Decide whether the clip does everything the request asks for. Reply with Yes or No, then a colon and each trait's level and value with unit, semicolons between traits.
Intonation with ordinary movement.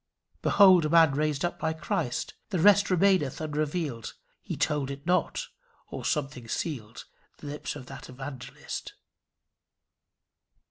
Yes: average, 3.9 semitones